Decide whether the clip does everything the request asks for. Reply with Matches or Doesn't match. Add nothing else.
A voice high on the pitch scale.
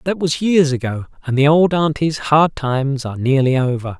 Doesn't match